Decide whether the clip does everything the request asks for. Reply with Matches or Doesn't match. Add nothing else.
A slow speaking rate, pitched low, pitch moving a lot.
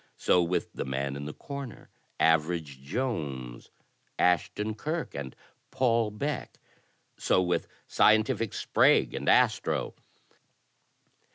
Matches